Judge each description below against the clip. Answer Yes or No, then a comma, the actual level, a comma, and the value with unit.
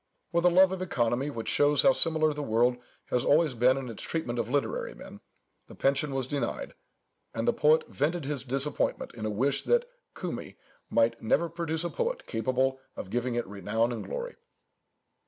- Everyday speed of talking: Yes, average, 185 wpm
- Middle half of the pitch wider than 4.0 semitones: Yes, average, 5.3 semitones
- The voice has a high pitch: No, low, 135 Hz